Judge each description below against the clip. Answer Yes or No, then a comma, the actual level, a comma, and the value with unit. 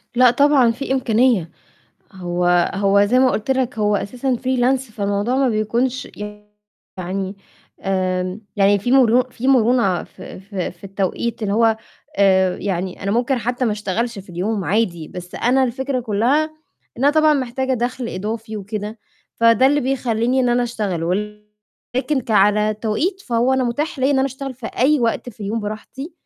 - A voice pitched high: Yes, high, 230 Hz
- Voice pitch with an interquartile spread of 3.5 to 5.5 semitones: Yes, average, 4.2 semitones